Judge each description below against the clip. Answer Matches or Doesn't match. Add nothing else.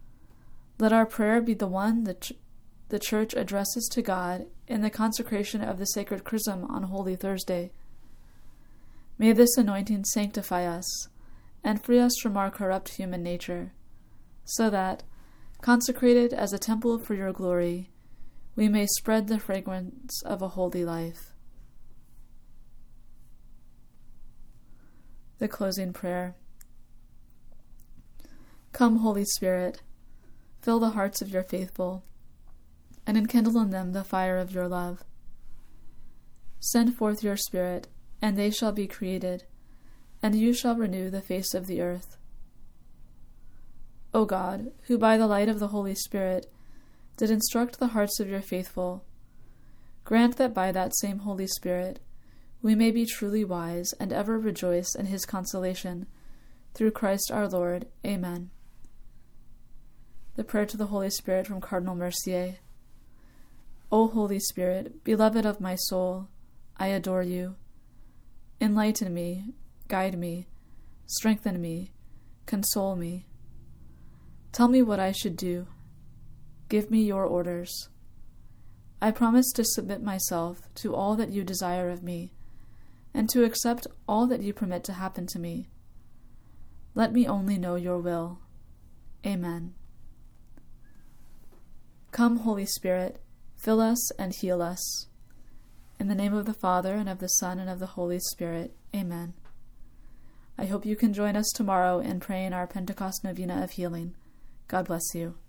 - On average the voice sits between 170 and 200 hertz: Matches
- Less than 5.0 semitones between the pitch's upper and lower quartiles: Matches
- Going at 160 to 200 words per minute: Doesn't match